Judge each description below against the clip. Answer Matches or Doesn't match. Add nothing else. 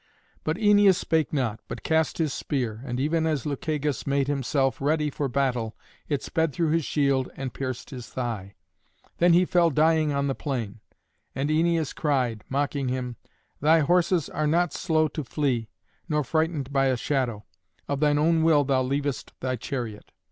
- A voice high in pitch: Doesn't match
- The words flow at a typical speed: Matches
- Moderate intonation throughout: Matches